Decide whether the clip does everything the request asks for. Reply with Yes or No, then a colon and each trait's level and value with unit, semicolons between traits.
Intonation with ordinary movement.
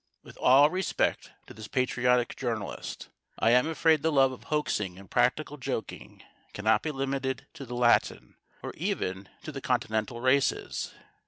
Yes: average, 3.4 semitones